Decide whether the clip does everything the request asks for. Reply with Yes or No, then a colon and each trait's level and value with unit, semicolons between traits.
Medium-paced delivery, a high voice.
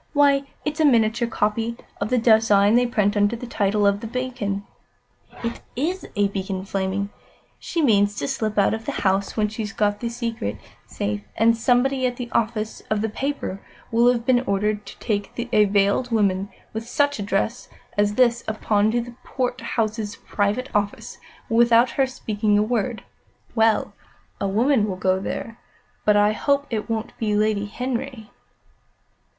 Yes: average, 165 wpm; high, 220 Hz